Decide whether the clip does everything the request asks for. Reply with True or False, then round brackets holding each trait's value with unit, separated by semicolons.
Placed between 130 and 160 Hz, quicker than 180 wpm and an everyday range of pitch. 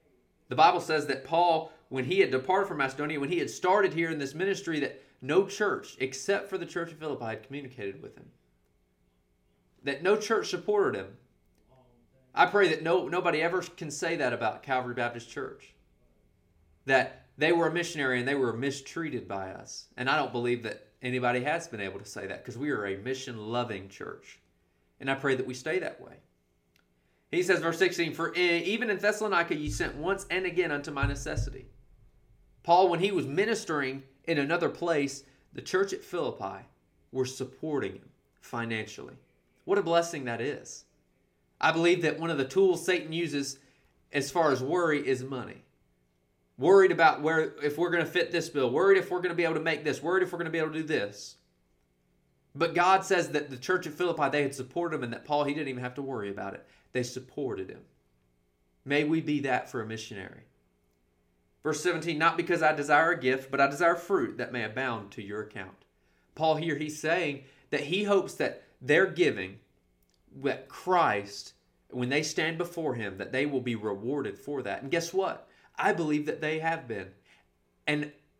False (140 Hz; 195 wpm; 7.0 semitones)